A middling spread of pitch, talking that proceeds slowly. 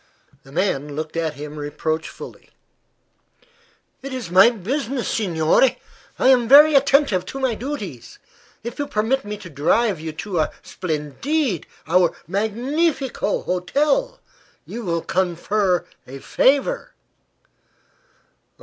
No: wide, 8.5 semitones; slow, 115 wpm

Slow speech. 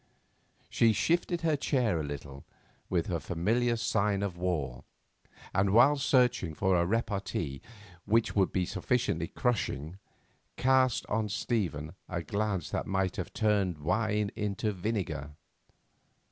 Yes: slow, 130 wpm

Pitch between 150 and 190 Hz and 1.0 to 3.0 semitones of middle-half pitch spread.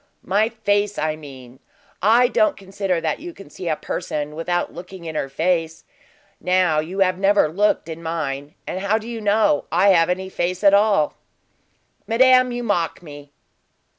No: medium, 185 Hz; average, 4.4 semitones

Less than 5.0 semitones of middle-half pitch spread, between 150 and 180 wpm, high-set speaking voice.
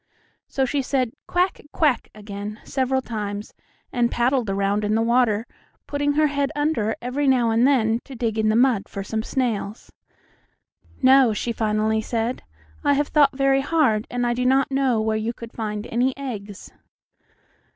Yes: average, 3.7 semitones; average, 170 wpm; high, 240 Hz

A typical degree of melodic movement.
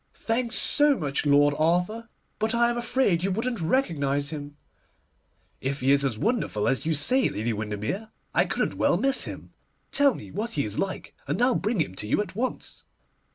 No: wide, 8.9 semitones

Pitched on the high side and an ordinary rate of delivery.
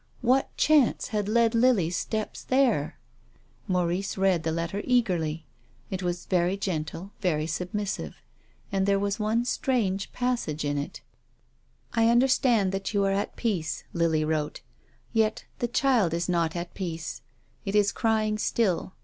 Yes: high, 195 Hz; average, 155 wpm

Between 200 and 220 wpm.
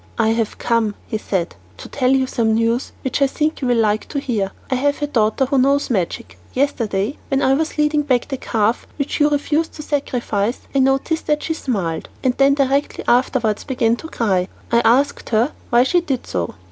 Yes: fast, 205 wpm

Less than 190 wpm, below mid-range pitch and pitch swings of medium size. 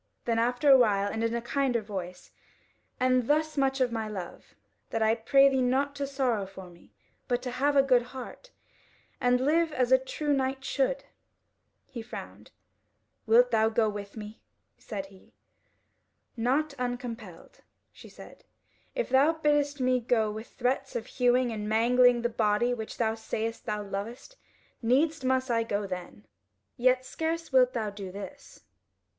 No: average, 165 wpm; high, 245 Hz; average, 3.5 semitones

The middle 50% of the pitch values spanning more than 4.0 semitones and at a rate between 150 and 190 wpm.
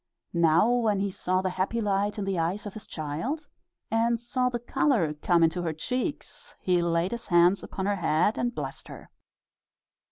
Yes: wide, 5.4 semitones; average, 185 wpm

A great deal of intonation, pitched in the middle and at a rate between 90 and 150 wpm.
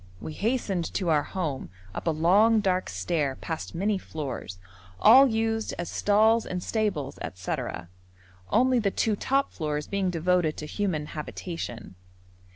Yes: wide, 5.8 semitones; medium, 180 Hz; average, 145 wpm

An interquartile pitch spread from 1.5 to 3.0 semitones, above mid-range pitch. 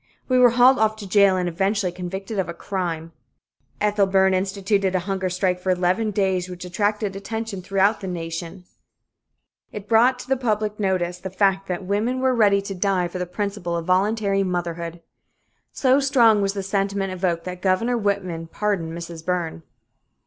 Yes: narrow, 2.6 semitones; high, 195 Hz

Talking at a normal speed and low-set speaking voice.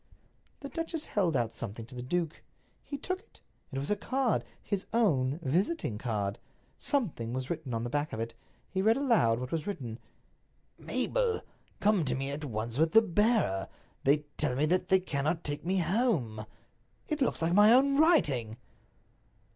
No: average, 170 wpm; medium, 160 Hz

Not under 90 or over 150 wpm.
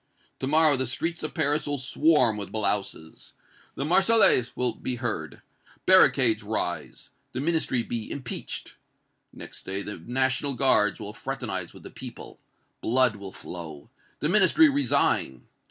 Yes: average, 140 wpm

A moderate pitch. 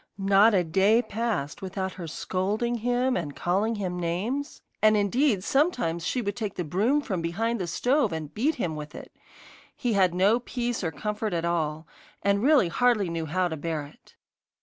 No: high, 200 Hz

